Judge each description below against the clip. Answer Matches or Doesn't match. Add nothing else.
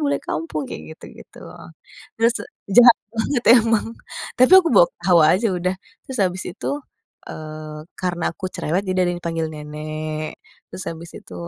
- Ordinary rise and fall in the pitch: Doesn't match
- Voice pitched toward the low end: Doesn't match